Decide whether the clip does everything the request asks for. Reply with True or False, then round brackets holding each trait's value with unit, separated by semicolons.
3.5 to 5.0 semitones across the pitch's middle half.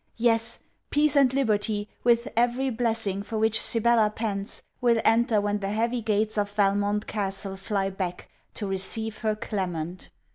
False (2.5 semitones)